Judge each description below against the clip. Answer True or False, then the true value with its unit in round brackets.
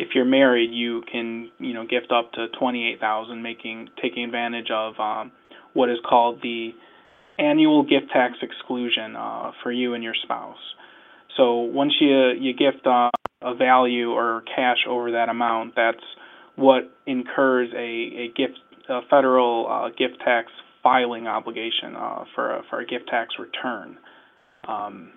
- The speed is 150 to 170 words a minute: True (155 wpm)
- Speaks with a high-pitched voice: False (120 Hz)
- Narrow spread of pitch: True (1.7 semitones)